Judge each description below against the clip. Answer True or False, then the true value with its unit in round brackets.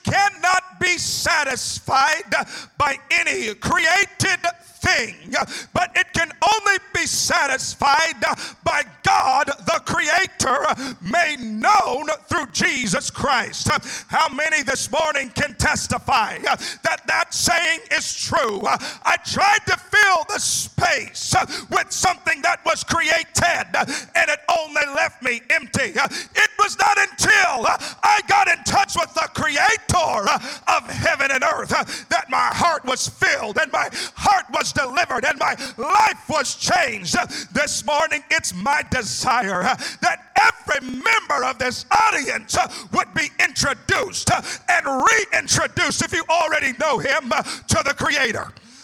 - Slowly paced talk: True (130 wpm)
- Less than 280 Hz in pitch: False (335 Hz)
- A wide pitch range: False (4.4 semitones)